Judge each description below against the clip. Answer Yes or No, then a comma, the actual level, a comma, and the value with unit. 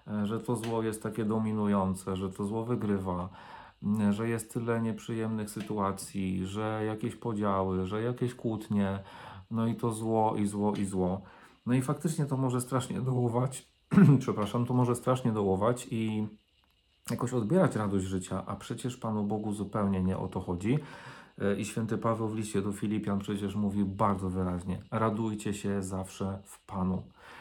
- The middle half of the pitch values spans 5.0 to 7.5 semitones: No, average, 2.9 semitones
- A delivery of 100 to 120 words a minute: No, average, 155 wpm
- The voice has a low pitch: Yes, low, 105 Hz